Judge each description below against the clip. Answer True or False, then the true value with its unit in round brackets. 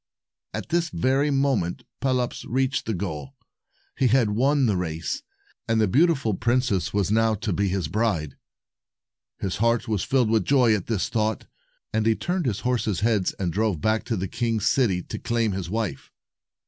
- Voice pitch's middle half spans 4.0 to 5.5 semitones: True (4.5 semitones)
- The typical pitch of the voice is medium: False (110 Hz)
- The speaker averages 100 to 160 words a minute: False (175 wpm)